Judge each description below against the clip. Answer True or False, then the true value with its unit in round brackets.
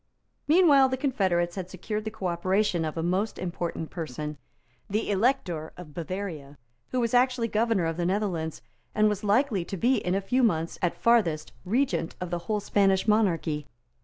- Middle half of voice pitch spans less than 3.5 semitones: False (4.8 semitones)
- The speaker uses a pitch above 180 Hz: True (190 Hz)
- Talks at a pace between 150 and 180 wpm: True (170 wpm)